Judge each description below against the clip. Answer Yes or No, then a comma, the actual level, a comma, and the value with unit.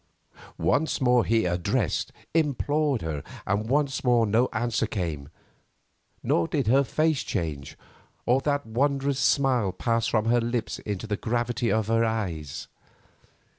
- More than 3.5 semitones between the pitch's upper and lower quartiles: Yes, average, 4.2 semitones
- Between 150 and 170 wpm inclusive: No, slow, 135 wpm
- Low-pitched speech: Yes, low, 115 Hz